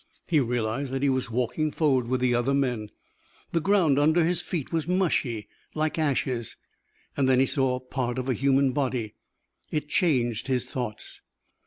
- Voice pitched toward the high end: No, low, 130 Hz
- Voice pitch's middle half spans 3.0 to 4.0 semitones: Yes, average, 3.6 semitones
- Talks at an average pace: Yes, average, 165 wpm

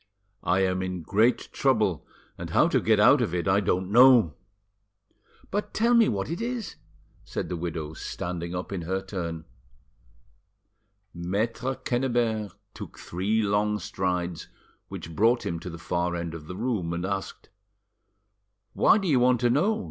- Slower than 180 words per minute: Yes, average, 160 wpm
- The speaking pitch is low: Yes, very low, 95 Hz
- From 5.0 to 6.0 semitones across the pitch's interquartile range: Yes, wide, 5.6 semitones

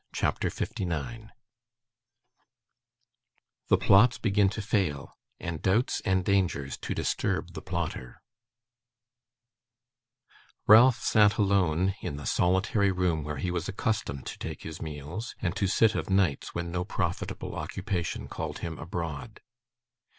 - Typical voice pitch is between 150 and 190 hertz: No, very low, 95 Hz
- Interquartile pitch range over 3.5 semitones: Yes, average, 4.0 semitones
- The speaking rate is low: Yes, slow, 125 wpm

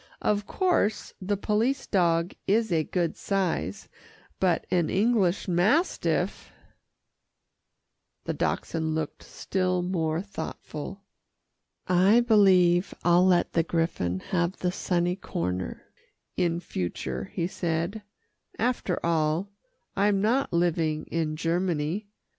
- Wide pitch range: No, average, 3.3 semitones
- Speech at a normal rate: No, slow, 110 wpm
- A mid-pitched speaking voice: Yes, medium, 180 Hz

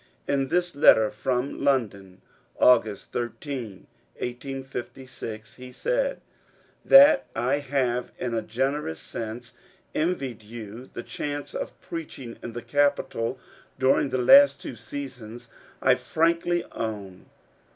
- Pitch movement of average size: Yes, average, 3.9 semitones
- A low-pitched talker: Yes, low, 125 Hz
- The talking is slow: Yes, slow, 120 wpm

